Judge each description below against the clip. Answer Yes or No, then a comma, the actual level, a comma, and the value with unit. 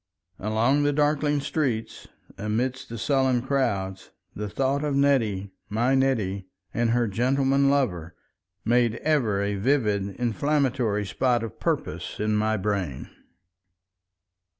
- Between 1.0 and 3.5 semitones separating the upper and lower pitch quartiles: No, average, 4.7 semitones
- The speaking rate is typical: No, slow, 120 wpm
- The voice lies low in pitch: Yes, low, 120 Hz